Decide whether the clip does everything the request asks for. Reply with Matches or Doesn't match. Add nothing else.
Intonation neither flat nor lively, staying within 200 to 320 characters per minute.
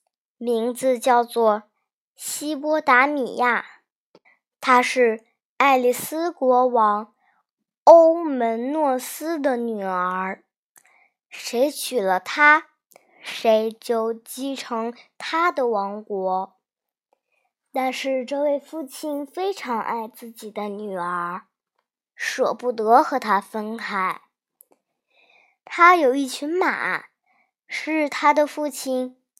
Doesn't match